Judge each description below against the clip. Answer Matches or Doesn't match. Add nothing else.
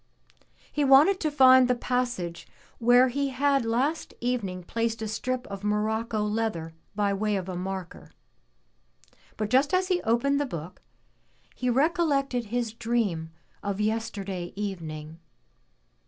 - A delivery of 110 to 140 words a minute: Matches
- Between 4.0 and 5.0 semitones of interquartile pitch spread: Matches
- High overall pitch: Matches